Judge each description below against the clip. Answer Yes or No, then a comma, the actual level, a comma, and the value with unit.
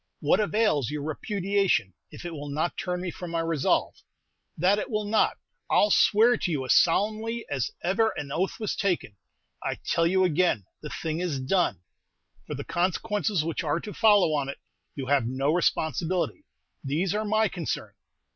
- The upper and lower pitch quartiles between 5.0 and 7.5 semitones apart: Yes, wide, 5.4 semitones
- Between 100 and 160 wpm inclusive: No, average, 180 wpm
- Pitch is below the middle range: No, medium, 175 Hz